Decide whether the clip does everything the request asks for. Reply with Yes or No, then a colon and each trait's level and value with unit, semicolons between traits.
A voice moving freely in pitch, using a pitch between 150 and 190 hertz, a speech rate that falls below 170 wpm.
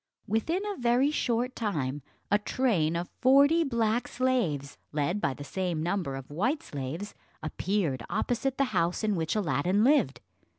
No: wide, 8.3 semitones; high, 205 Hz; average, 155 wpm